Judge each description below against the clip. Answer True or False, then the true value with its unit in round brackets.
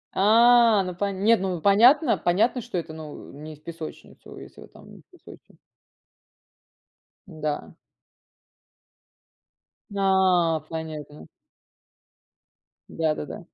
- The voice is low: False (185 Hz)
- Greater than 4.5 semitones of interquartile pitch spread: True (4.9 semitones)